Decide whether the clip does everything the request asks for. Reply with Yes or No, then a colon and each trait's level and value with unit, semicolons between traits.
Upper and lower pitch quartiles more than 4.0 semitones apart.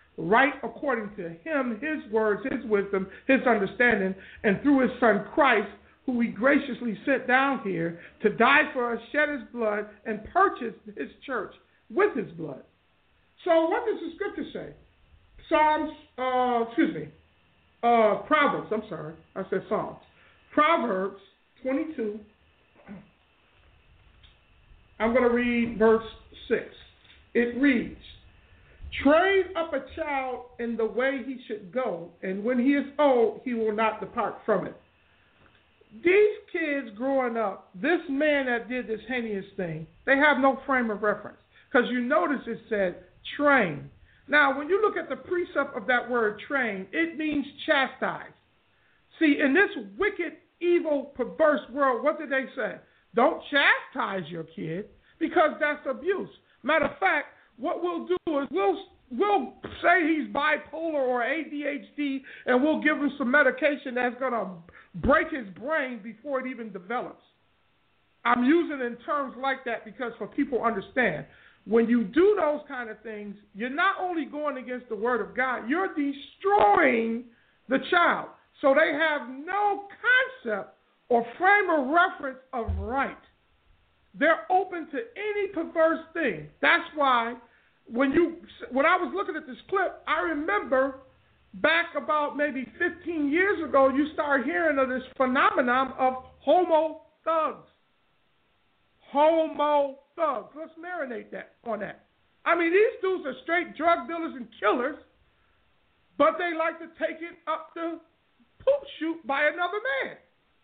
Yes: average, 5.1 semitones